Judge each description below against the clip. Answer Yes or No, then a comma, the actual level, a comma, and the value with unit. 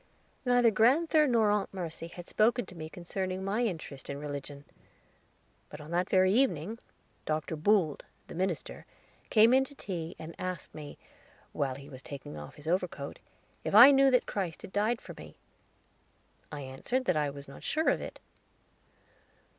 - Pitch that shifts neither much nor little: No, wide, 6.9 semitones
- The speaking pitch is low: No, medium, 180 Hz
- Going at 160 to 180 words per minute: Yes, average, 170 wpm